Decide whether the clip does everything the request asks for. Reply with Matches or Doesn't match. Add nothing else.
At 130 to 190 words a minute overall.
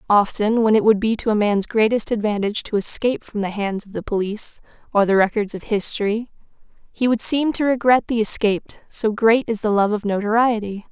Doesn't match